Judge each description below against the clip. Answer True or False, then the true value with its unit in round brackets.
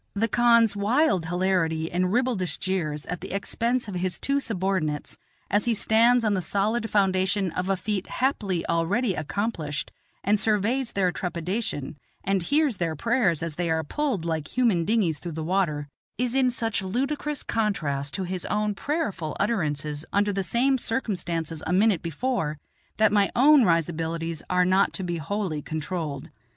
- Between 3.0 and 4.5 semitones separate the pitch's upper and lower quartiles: False (5.3 semitones)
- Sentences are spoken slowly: False (165 wpm)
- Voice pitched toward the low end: False (190 Hz)